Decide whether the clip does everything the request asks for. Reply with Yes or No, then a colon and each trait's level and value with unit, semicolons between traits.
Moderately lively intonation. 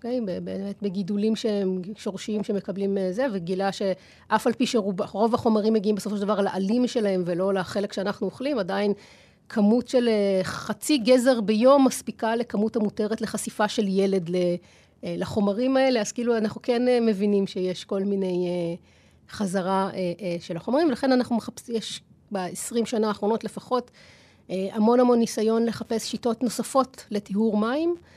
Yes: average, 3.1 semitones